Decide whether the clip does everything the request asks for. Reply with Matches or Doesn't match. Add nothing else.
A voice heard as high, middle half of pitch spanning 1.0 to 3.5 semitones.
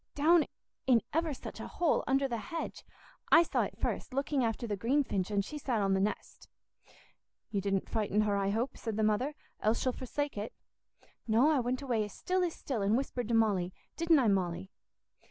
Doesn't match